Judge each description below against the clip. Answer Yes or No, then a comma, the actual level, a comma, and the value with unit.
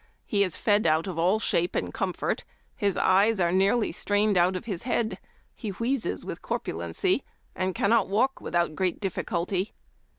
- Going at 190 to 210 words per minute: No, average, 170 wpm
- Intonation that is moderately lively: Yes, average, 3.2 semitones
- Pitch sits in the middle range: No, high, 195 Hz